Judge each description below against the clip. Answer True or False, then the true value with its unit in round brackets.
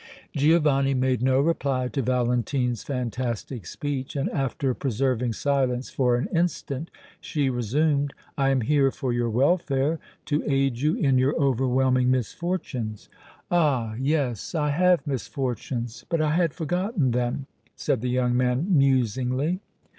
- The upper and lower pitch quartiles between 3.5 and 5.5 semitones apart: False (2.9 semitones)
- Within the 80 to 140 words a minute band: True (135 wpm)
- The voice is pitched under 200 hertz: True (135 Hz)